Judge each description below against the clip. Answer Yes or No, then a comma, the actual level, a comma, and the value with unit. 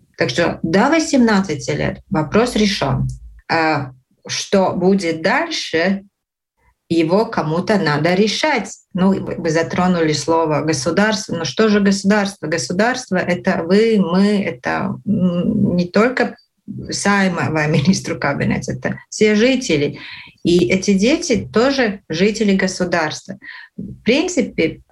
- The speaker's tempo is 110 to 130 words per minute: Yes, average, 115 wpm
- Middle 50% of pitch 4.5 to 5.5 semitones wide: Yes, average, 4.8 semitones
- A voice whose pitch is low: No, high, 195 Hz